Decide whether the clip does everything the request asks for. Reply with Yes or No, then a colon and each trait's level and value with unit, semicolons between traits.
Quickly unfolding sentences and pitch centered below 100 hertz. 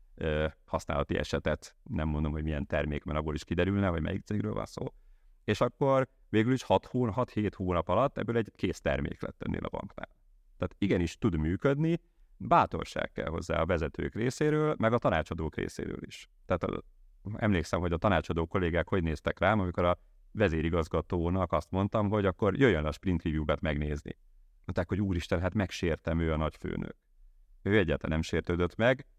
Yes: fast, 165 wpm; very low, 90 Hz